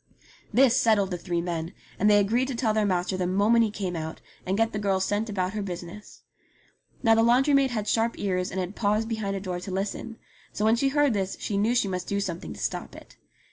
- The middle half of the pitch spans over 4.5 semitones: No, average, 3.3 semitones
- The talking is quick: Yes, fast, 240 wpm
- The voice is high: Yes, high, 205 Hz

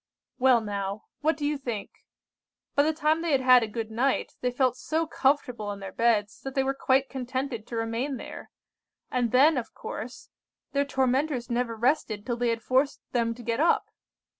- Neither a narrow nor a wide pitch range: Yes, average, 3.2 semitones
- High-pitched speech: Yes, very high, 250 Hz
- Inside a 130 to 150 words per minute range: No, average, 190 wpm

